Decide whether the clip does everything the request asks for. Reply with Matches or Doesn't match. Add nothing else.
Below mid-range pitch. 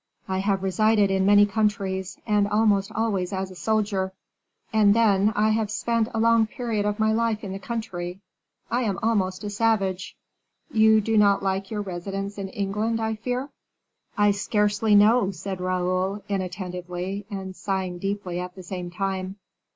Doesn't match